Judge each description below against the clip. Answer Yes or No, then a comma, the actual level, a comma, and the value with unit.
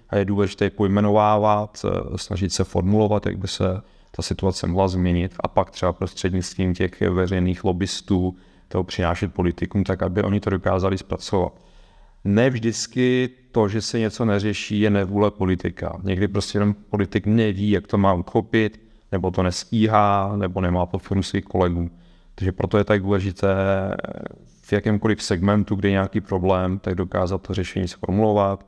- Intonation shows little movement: Yes, narrow, 1.9 semitones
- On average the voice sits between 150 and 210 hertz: No, low, 100 Hz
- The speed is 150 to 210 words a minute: Yes, average, 155 wpm